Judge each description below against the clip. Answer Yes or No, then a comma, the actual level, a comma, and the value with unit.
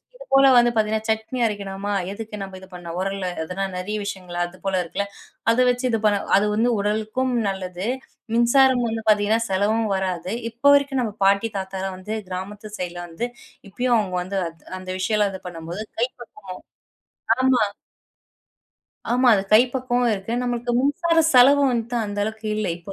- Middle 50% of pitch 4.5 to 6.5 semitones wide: No, average, 4.0 semitones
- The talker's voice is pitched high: Yes, high, 210 Hz